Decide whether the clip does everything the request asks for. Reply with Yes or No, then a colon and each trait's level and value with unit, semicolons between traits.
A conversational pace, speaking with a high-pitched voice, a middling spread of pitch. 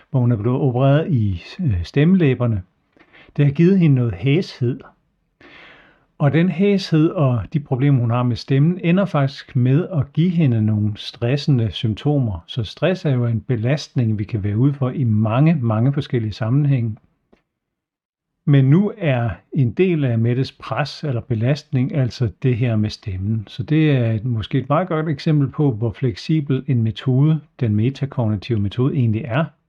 No: average, 165 wpm; low, 135 Hz; average, 4.2 semitones